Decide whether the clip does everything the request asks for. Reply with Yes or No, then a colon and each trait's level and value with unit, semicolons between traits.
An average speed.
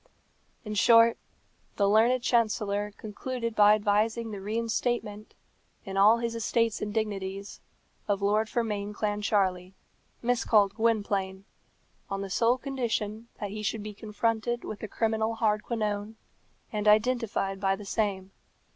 No: slow, 130 wpm